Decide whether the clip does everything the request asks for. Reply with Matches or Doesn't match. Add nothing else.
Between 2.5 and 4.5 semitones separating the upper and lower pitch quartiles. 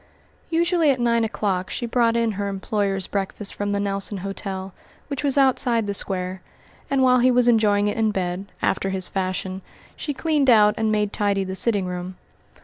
Matches